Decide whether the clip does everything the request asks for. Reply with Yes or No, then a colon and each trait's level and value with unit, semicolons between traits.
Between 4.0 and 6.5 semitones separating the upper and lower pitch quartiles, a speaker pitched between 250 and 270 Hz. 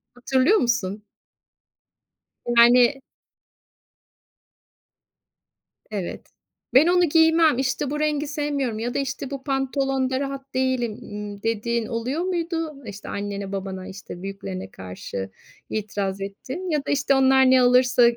Yes: average, 5.2 semitones; very high, 255 Hz